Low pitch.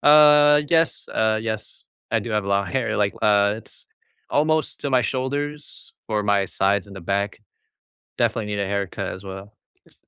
Yes: low, 105 Hz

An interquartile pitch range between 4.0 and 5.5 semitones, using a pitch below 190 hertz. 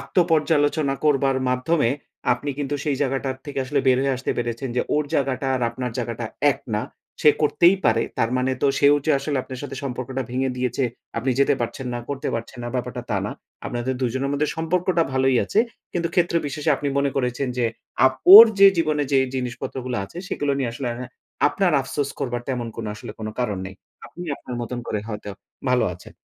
No: average, 2.9 semitones; low, 135 Hz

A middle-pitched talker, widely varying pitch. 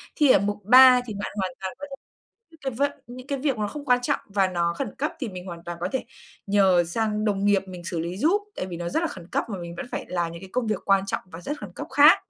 No: high, 200 Hz; wide, 5.9 semitones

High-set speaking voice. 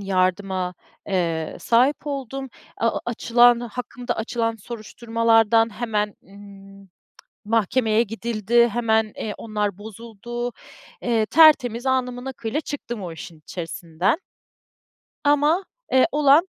Yes: high, 230 Hz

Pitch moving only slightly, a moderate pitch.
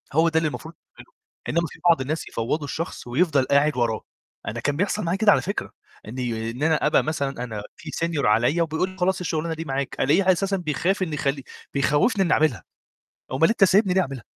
No: average, 4.7 semitones; medium, 155 Hz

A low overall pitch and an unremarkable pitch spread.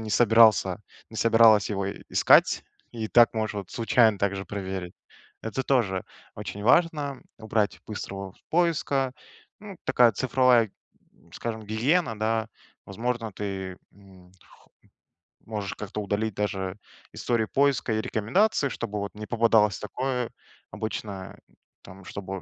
Yes: low, 110 Hz; average, 3.1 semitones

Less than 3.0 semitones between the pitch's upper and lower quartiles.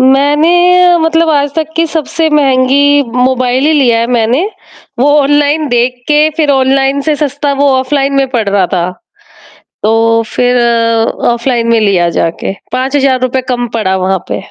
No: average, 3.6 semitones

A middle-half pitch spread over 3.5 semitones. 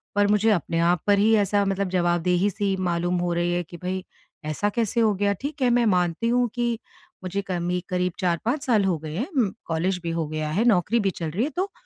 Yes: average, 4.2 semitones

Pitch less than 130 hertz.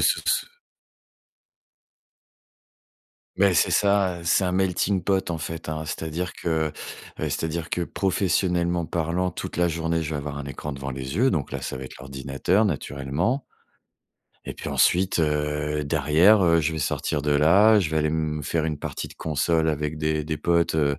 Yes: very low, 80 Hz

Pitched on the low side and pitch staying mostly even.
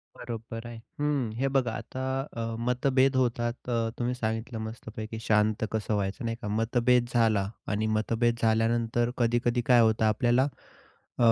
Yes: low, 115 Hz; narrow, 1.7 semitones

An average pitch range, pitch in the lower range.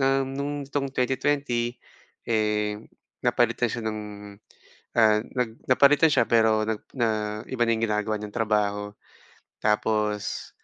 Yes: average, 3.2 semitones; low, 110 Hz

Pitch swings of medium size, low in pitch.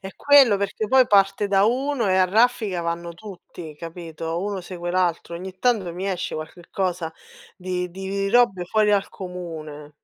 No: average, 3.0 semitones; medium, 185 Hz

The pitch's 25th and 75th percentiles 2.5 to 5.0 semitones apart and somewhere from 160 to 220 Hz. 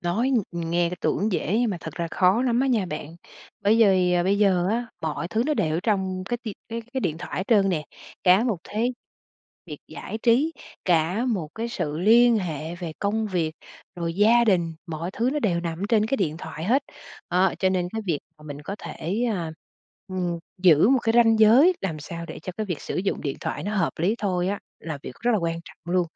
Yes: average, 4.7 semitones; high, 190 Hz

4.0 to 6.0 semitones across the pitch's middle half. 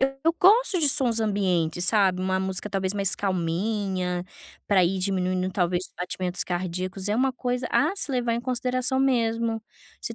Yes: average, 5.2 semitones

